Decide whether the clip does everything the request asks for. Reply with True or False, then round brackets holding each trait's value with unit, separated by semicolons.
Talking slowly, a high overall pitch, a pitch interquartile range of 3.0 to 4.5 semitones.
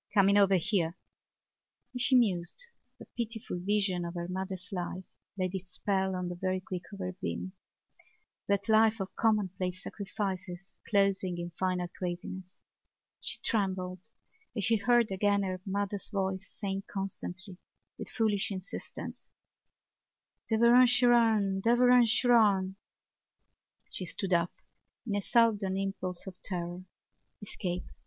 False (125 wpm; 195 Hz; 2.4 semitones)